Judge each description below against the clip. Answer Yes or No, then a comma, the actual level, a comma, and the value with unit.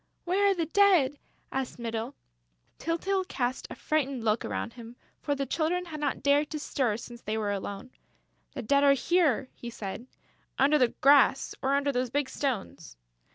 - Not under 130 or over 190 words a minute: Yes, average, 175 wpm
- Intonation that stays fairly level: No, average, 4.4 semitones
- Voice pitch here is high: Yes, very high, 275 Hz